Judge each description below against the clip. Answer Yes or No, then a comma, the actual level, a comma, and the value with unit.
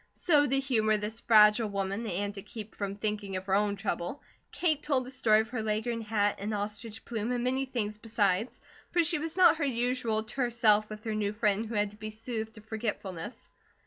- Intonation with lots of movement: No, average, 2.7 semitones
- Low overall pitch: No, high, 220 Hz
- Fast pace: Yes, fast, 210 wpm